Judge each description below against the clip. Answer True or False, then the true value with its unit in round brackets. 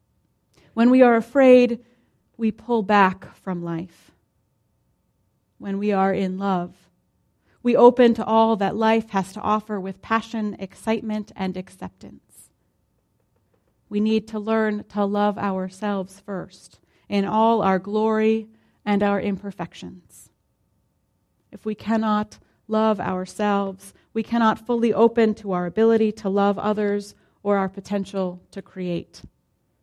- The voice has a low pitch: False (205 Hz)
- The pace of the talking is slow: True (125 wpm)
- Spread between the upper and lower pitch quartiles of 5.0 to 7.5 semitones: False (2.4 semitones)